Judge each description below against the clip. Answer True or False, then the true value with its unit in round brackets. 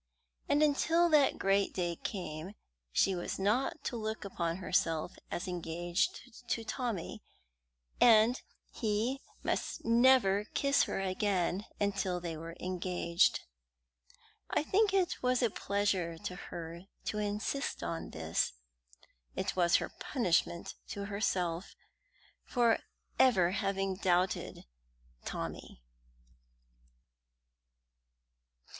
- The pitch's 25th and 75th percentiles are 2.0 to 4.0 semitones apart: False (4.9 semitones)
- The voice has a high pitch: True (195 Hz)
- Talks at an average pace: False (105 wpm)